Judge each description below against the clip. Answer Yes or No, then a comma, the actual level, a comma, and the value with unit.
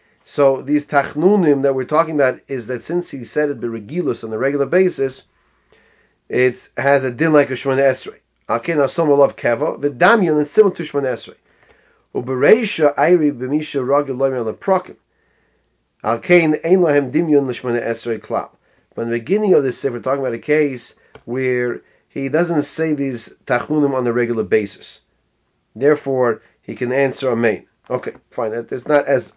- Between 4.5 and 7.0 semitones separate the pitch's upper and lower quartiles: No, average, 3.0 semitones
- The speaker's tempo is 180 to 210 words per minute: No, average, 160 wpm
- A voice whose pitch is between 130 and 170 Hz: Yes, medium, 140 Hz